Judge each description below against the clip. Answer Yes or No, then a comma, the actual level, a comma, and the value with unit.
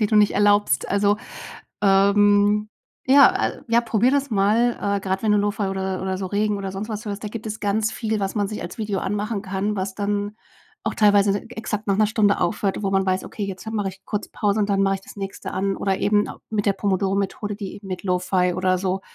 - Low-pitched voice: No, high, 205 Hz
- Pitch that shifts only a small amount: Yes, narrow, 1.5 semitones